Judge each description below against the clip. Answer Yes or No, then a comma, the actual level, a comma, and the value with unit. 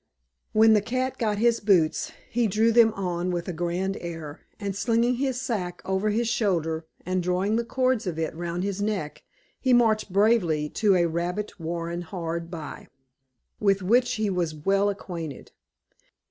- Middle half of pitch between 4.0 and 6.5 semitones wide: Yes, average, 4.4 semitones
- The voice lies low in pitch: No, high, 195 Hz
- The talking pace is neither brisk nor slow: Yes, average, 165 wpm